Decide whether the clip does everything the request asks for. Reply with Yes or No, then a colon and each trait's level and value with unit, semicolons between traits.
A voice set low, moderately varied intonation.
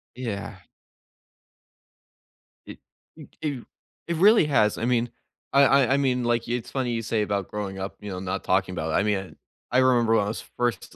Yes: low, 115 Hz; average, 4.0 semitones